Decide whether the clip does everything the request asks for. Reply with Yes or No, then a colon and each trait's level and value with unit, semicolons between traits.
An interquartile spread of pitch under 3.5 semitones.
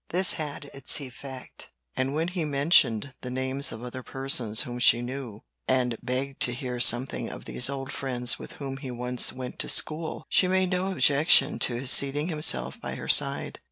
Yes: average, 2.9 semitones